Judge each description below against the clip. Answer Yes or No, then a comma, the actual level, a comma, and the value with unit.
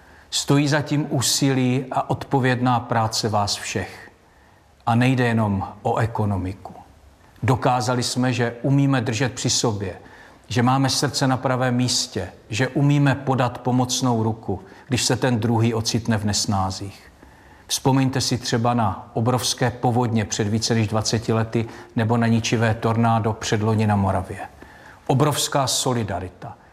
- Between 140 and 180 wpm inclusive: No, average, 130 wpm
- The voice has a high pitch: No, low, 120 Hz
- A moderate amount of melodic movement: Yes, average, 3.0 semitones